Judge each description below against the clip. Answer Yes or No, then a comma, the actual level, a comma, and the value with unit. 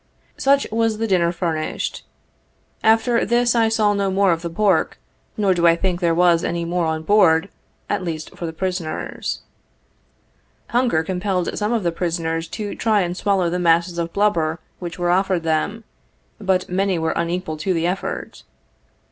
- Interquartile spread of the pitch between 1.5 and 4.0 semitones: Yes, average, 3.5 semitones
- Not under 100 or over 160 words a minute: No, average, 175 wpm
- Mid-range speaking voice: Yes, medium, 180 Hz